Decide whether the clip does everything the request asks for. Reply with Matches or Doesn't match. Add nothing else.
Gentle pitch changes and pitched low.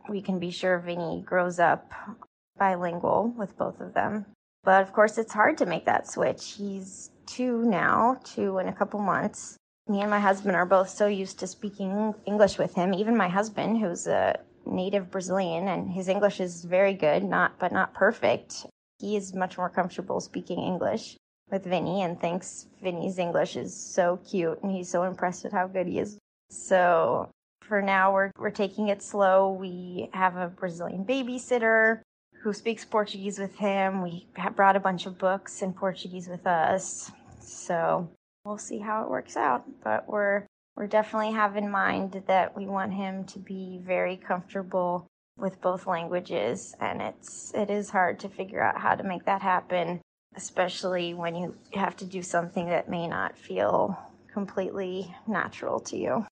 Doesn't match